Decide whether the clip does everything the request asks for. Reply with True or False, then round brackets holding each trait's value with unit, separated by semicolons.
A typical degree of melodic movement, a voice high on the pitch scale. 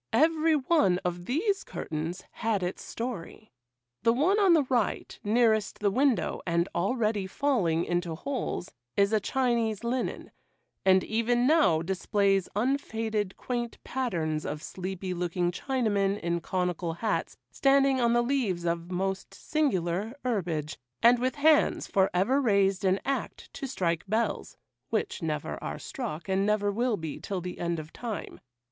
False (5.9 semitones; 205 Hz)